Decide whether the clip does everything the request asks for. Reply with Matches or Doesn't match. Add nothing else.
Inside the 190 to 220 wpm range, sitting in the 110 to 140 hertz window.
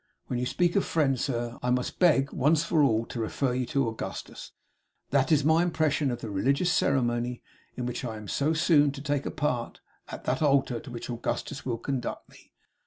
Matches